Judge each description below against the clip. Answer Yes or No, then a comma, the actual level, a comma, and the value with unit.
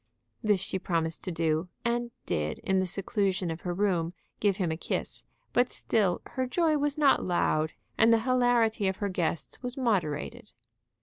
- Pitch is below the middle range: No, high, 195 Hz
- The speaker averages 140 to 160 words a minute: No, average, 175 wpm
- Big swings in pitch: Yes, wide, 5.7 semitones